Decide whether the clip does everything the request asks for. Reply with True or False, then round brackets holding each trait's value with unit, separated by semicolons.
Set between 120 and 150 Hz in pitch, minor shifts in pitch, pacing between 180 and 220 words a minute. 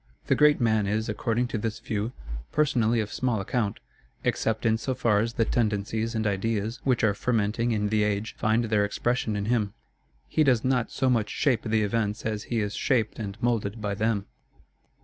False (110 Hz; 2.2 semitones; 190 wpm)